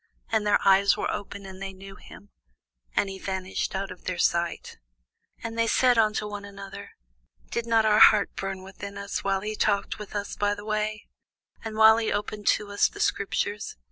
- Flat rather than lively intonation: Yes, narrow, 1.7 semitones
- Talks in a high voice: Yes, high, 205 Hz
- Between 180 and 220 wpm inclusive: Yes, average, 195 wpm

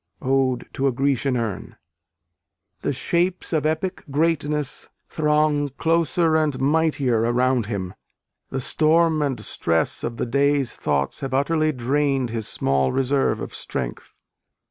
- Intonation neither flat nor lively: Yes, average, 4.1 semitones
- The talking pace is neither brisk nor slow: No, slow, 130 wpm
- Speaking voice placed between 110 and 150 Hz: Yes, medium, 140 Hz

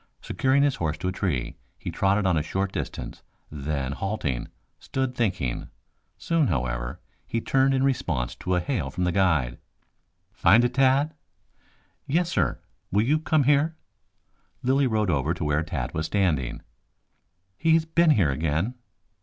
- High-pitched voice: No, very low, 95 Hz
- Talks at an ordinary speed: Yes, average, 155 wpm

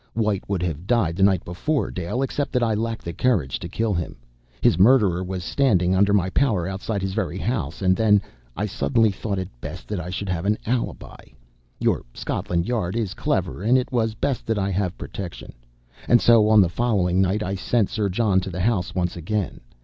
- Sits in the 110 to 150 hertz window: No, low, 100 Hz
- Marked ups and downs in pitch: No, average, 3.7 semitones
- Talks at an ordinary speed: No, fast, 210 wpm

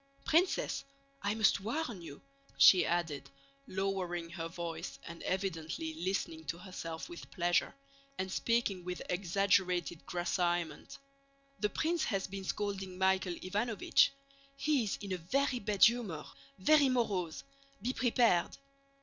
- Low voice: No, high, 190 Hz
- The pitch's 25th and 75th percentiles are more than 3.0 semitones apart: Yes, average, 3.7 semitones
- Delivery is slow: Yes, slow, 125 wpm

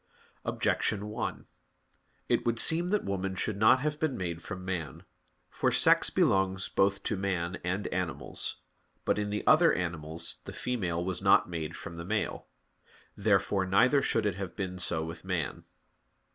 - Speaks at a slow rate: No, average, 160 wpm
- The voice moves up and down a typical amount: Yes, average, 3.2 semitones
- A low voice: Yes, very low, 95 Hz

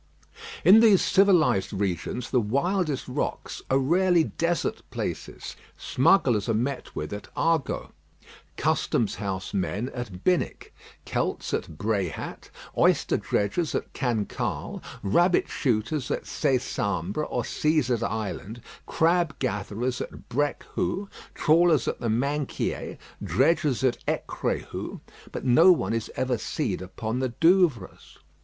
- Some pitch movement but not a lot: No, wide, 7.2 semitones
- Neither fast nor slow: No, slow, 120 wpm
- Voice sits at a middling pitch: No, low, 130 Hz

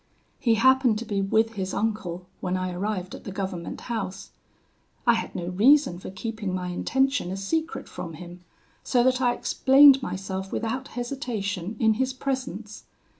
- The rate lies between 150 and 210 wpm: Yes, average, 165 wpm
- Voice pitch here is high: Yes, high, 215 Hz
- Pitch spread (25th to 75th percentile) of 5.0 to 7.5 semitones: Yes, average, 5.3 semitones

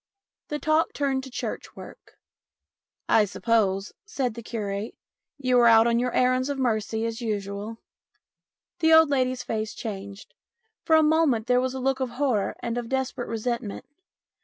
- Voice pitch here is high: Yes, high, 245 Hz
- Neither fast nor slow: Yes, average, 180 wpm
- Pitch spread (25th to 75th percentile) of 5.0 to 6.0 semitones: No, average, 3.2 semitones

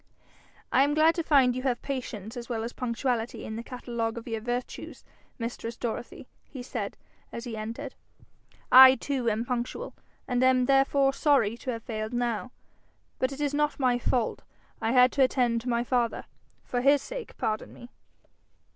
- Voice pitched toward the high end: Yes, high, 245 Hz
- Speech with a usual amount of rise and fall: No, narrow, 2.3 semitones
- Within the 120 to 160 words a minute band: No, average, 175 wpm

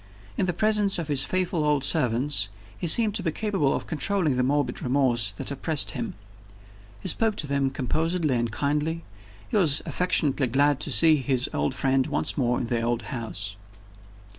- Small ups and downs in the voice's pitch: No, average, 4.7 semitones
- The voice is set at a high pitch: No, medium, 145 Hz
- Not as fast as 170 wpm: No, average, 180 wpm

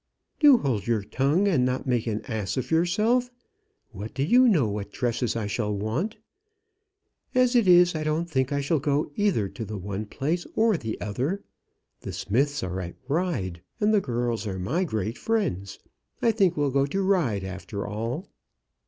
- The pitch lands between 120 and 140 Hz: Yes, low, 135 Hz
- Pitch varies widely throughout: Yes, wide, 8.8 semitones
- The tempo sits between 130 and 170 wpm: No, average, 180 wpm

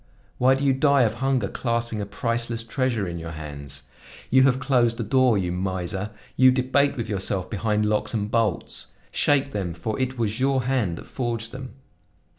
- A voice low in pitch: Yes, low, 115 Hz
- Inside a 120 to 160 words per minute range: No, average, 185 wpm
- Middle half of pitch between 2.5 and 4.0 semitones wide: No, average, 4.5 semitones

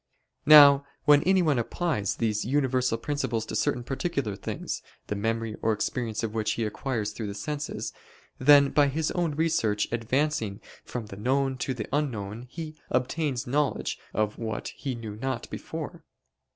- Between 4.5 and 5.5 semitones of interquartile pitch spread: Yes, average, 4.9 semitones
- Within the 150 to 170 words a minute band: Yes, average, 155 wpm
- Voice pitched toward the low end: Yes, low, 125 Hz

